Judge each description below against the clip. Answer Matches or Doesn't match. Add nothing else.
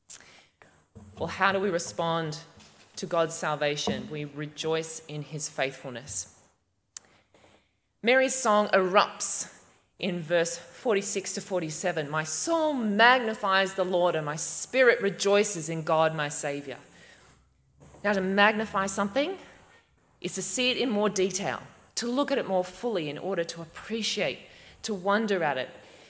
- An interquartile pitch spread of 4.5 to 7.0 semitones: Matches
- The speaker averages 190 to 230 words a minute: Doesn't match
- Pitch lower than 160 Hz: Doesn't match